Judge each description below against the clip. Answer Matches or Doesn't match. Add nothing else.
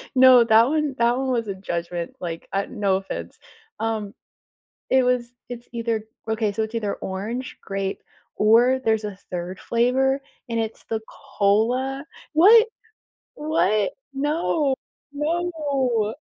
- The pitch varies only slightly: Doesn't match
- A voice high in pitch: Matches